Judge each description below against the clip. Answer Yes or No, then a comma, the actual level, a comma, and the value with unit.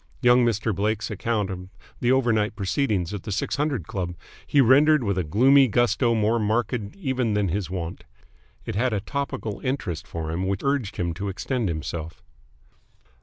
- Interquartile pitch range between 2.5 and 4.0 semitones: No, average, 4.8 semitones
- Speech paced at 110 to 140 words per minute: No, average, 170 wpm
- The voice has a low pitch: Yes, low, 105 Hz